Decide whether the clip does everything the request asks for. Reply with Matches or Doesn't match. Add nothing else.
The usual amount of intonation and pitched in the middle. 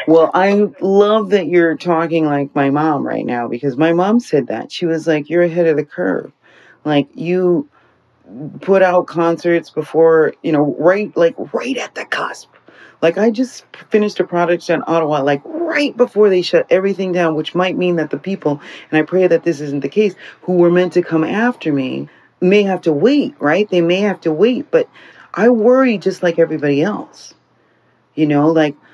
Matches